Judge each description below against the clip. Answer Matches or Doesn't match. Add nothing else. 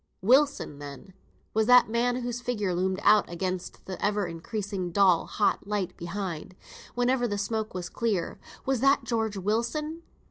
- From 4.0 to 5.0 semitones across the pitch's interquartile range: Matches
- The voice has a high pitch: Matches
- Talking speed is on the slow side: Doesn't match